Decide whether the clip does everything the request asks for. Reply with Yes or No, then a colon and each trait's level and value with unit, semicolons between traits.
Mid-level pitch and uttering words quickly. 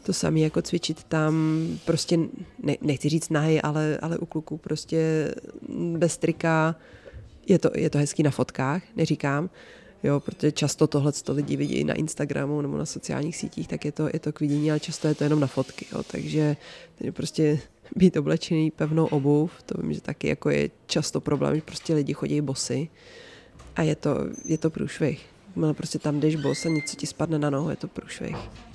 Yes: medium, 155 Hz; fast, 195 wpm